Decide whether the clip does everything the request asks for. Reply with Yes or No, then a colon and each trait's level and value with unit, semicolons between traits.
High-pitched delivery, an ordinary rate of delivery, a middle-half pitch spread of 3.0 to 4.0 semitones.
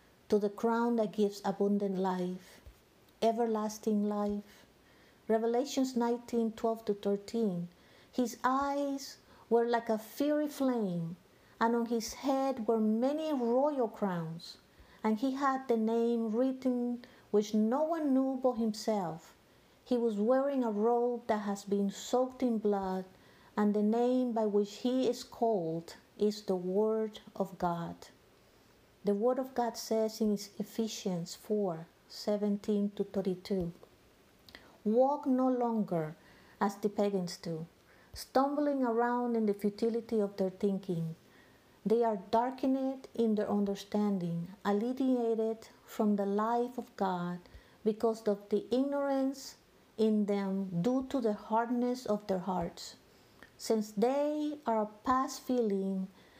No: high, 220 Hz; slow, 130 wpm; average, 3.3 semitones